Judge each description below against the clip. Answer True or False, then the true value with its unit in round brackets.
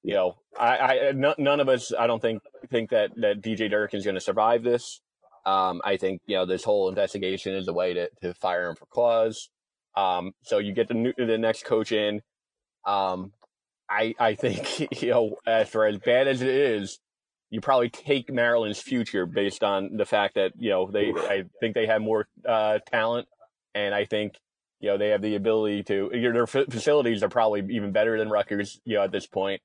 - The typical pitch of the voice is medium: False (110 Hz)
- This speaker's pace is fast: True (210 wpm)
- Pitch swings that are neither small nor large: True (3.0 semitones)